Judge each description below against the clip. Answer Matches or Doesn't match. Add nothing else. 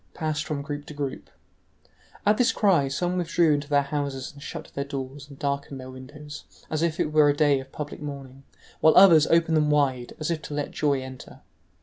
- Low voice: Doesn't match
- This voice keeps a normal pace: Doesn't match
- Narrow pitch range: Matches